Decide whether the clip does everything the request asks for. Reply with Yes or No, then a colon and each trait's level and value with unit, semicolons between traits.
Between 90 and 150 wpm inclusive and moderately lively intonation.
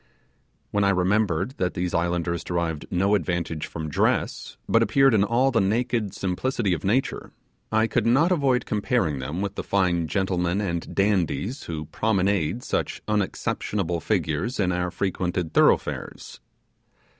Yes: average, 145 wpm; average, 4.0 semitones